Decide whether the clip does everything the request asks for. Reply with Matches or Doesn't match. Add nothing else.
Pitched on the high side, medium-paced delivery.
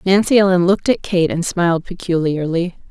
Doesn't match